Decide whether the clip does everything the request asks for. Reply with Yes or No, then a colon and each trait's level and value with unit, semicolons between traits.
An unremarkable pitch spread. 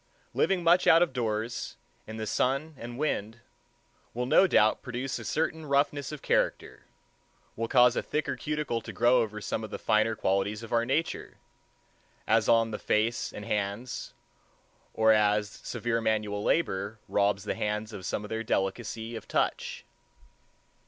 Yes: average, 3.3 semitones